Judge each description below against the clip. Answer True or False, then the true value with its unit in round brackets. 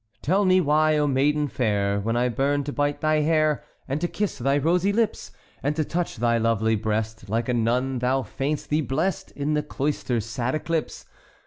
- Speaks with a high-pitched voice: False (140 Hz)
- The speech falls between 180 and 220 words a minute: True (195 wpm)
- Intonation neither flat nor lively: True (4.5 semitones)